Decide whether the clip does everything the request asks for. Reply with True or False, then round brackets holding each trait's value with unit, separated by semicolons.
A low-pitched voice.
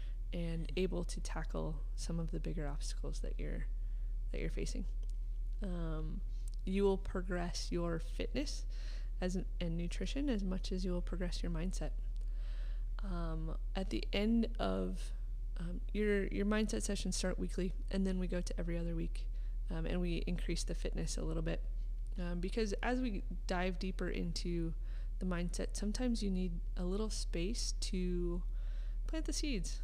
False (170 Hz)